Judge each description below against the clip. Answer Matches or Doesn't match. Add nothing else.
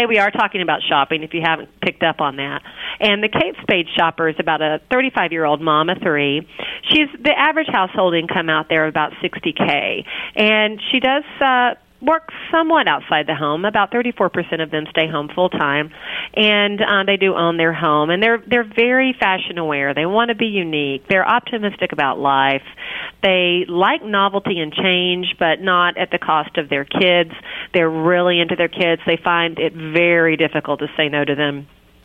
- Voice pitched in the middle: Matches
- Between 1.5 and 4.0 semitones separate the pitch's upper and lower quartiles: Doesn't match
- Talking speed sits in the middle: Matches